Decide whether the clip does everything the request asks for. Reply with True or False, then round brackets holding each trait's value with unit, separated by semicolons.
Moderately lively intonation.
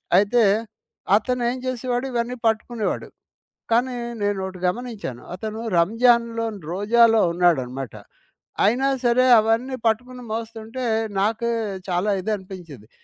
True (3.7 semitones)